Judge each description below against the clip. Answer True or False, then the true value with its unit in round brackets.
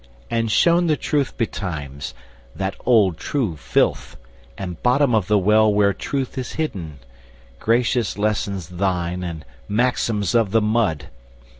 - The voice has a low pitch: True (105 Hz)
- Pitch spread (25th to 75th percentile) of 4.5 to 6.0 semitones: True (4.8 semitones)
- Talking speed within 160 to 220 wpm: False (135 wpm)